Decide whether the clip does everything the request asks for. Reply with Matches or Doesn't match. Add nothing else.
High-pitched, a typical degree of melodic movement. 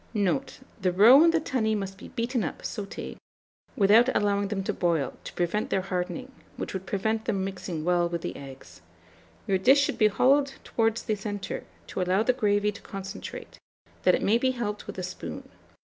Matches